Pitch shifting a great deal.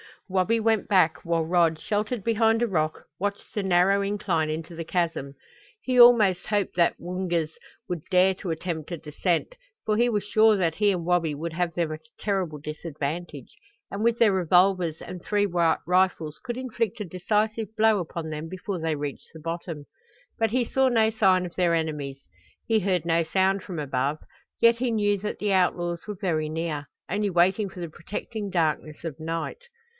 No: average, 4.2 semitones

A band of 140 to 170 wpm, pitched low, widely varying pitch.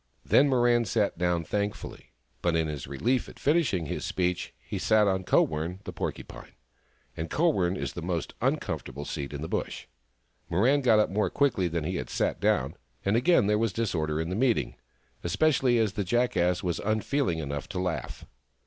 No: average, 185 wpm; very low, 95 Hz; wide, 5.9 semitones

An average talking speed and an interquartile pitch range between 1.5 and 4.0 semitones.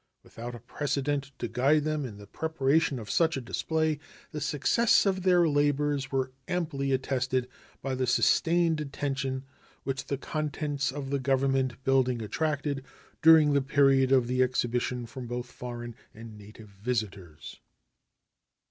Yes: average, 145 wpm; average, 2.9 semitones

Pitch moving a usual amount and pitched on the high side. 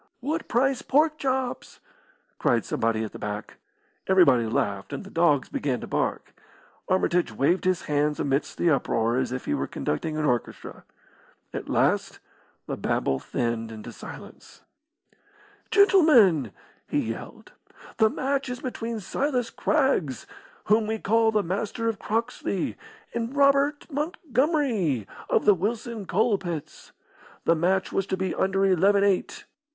No: wide, 9.0 semitones; high, 195 Hz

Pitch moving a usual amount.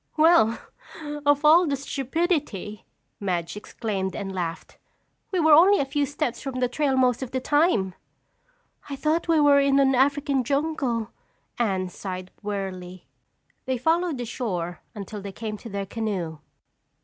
No: wide, 6.5 semitones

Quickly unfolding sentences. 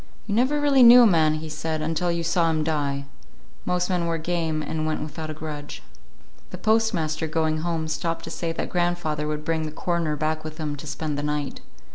Yes: fast, 210 wpm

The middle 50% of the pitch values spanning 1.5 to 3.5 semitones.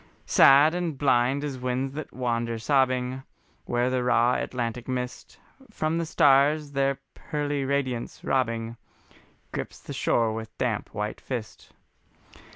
Yes: average, 2.8 semitones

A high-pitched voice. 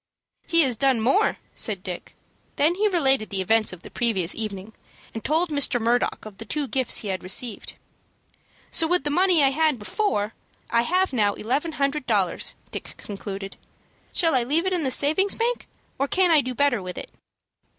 Yes: very high, 260 Hz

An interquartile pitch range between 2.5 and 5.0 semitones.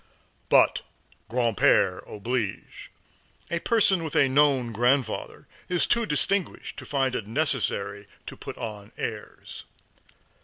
No: wide, 5.5 semitones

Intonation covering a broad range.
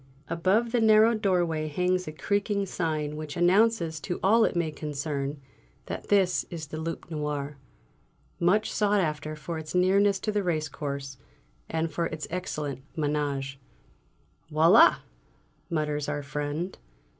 No: average, 4.0 semitones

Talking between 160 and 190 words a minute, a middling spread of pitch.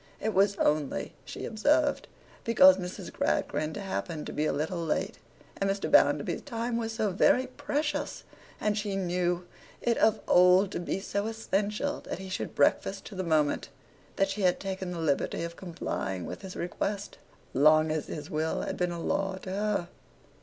Yes: average, 175 wpm; average, 3.9 semitones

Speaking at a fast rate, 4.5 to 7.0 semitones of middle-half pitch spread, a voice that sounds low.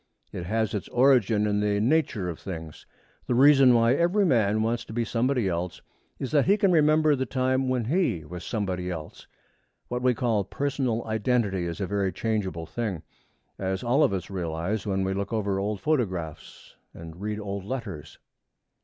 No: average, 180 wpm; average, 5.1 semitones; low, 110 Hz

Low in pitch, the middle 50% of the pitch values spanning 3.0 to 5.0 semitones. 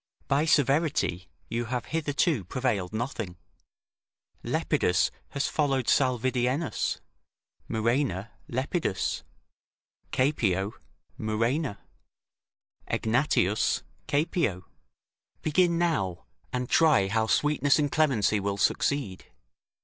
No: low, 125 Hz; wide, 5.5 semitones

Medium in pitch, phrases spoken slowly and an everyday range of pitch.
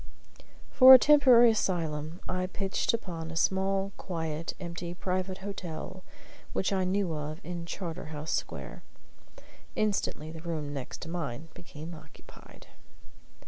Yes: medium, 175 Hz; slow, 120 wpm; average, 3.3 semitones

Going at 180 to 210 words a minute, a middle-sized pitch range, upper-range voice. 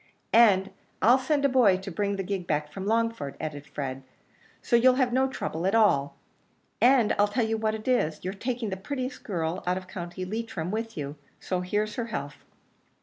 Yes: average, 200 wpm; average, 4.7 semitones; high, 205 Hz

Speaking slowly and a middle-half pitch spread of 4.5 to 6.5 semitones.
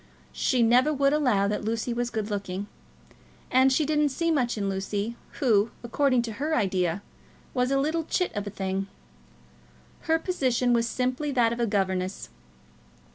No: average, 165 wpm; average, 5.2 semitones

